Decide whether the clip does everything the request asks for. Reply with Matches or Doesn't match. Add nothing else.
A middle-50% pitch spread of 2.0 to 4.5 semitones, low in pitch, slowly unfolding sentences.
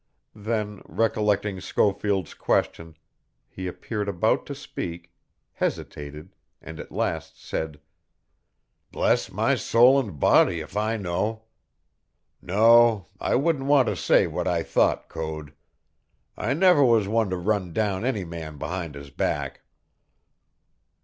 Doesn't match